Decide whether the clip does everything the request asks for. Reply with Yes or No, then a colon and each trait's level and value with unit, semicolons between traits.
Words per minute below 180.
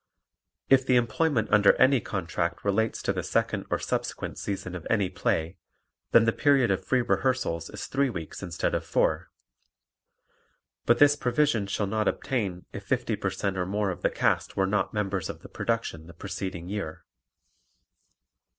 Yes: average, 170 wpm